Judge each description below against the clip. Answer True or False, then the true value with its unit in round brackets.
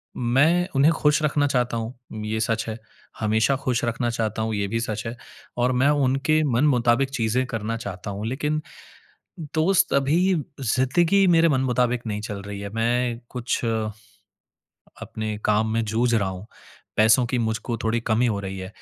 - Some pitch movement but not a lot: True (3.5 semitones)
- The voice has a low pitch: True (120 Hz)